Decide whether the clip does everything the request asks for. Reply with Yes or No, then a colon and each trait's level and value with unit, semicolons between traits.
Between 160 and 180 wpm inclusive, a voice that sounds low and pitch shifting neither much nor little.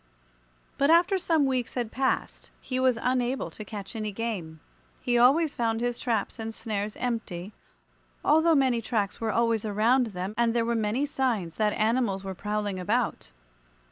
No: average, 165 wpm; high, 230 Hz; average, 3.4 semitones